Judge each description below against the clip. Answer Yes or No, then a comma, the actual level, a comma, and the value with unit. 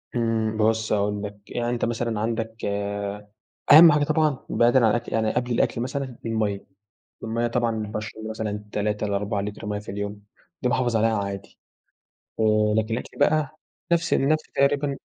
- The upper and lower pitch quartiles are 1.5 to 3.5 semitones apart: Yes, average, 2.7 semitones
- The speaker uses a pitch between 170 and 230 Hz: No, low, 115 Hz